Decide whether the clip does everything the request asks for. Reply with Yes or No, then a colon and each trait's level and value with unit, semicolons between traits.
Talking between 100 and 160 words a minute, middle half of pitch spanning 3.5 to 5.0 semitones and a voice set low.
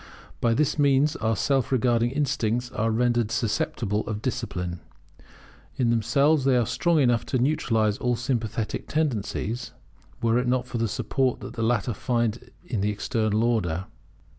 No: average, 155 wpm; average, 2.8 semitones; low, 120 Hz